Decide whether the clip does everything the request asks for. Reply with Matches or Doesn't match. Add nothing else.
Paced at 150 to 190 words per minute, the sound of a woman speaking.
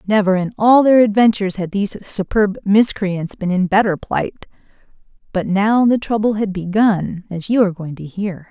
Matches